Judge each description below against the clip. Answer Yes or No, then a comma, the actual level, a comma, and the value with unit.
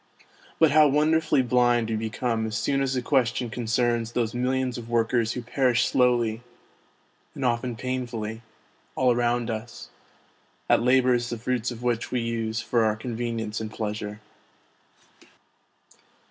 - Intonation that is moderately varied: No, narrow, 1.9 semitones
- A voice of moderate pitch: No, low, 120 Hz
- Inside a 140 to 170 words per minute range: Yes, average, 145 wpm